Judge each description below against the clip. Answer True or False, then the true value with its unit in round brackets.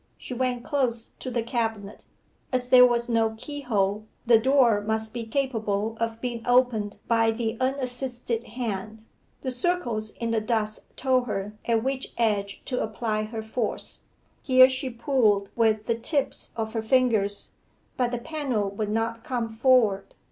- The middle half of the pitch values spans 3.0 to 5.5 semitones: False (2.4 semitones)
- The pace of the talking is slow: False (155 wpm)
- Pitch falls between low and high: False (230 Hz)